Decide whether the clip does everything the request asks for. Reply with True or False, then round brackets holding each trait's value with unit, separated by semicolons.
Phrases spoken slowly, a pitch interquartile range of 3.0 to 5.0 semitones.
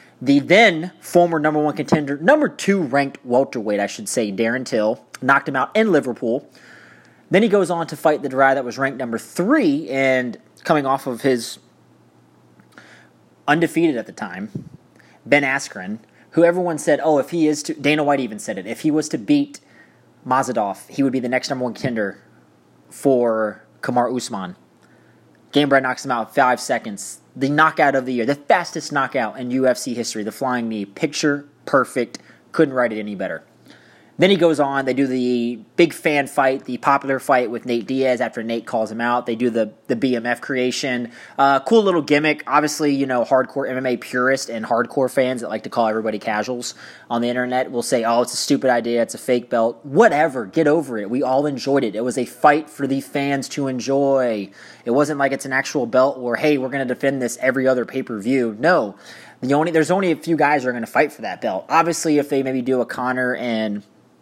False (205 wpm; 3.4 semitones)